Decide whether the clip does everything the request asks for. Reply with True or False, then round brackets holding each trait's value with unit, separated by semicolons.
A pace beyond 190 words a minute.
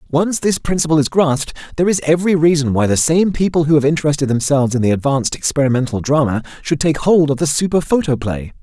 True (200 wpm)